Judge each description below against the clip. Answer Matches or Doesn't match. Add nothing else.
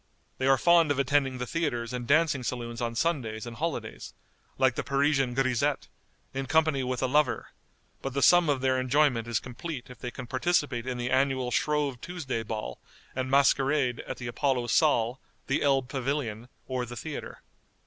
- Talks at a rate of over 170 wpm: Matches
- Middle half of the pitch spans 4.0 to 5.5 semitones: Doesn't match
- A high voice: Doesn't match